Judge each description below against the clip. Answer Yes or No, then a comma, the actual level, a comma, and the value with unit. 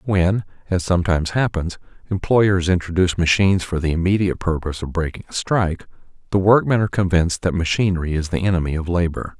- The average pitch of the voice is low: Yes, very low, 90 Hz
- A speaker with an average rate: Yes, average, 165 wpm